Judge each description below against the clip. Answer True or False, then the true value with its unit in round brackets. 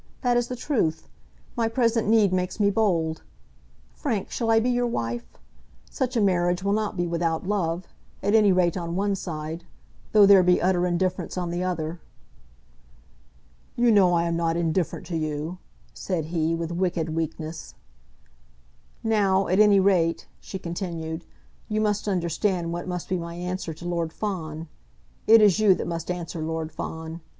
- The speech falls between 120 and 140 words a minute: False (165 wpm)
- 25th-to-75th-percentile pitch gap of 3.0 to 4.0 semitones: True (3.4 semitones)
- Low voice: False (180 Hz)